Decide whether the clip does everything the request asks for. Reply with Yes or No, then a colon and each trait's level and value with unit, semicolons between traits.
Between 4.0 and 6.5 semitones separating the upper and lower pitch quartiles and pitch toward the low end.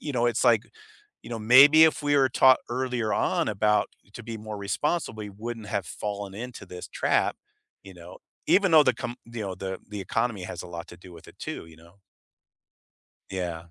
Yes: average, 4.6 semitones; low, 110 Hz